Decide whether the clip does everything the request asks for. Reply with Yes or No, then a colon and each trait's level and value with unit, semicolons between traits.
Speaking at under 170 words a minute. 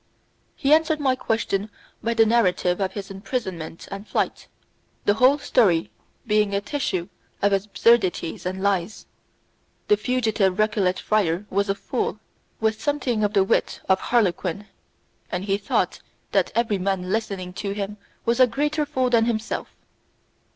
Yes: average, 150 wpm